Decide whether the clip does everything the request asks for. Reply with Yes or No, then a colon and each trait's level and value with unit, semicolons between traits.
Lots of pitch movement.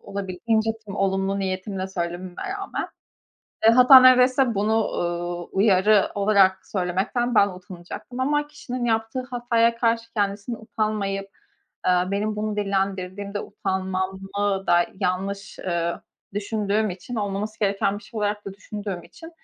No: average, 2.8 semitones